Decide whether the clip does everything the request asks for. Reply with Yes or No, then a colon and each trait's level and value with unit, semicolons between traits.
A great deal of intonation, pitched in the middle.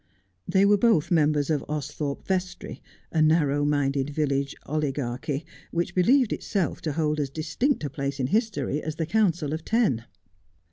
No: average, 3.8 semitones; medium, 155 Hz